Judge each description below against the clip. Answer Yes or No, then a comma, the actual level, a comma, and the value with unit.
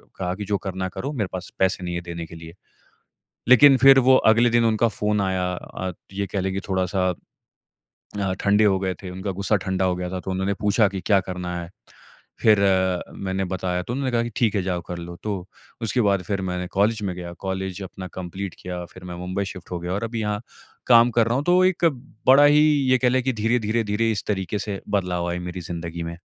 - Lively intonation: No, average, 3.7 semitones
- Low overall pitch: Yes, very low, 95 Hz